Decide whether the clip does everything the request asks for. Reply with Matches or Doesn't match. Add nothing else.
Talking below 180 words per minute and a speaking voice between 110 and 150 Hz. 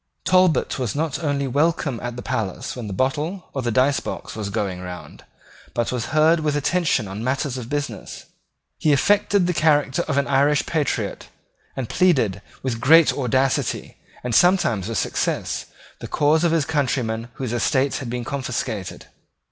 Matches